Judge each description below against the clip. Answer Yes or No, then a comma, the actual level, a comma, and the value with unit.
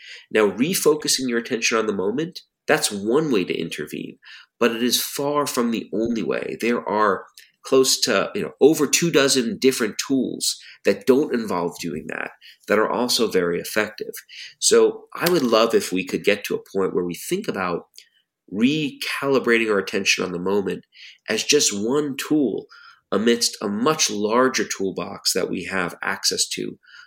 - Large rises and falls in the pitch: Yes, wide, 9.0 semitones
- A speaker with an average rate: Yes, average, 170 wpm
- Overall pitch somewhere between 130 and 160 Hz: Yes, low, 135 Hz